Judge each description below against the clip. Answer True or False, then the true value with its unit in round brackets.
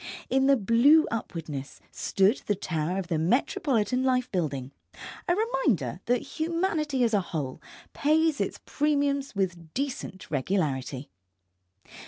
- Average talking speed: False (125 wpm)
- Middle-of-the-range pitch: False (225 Hz)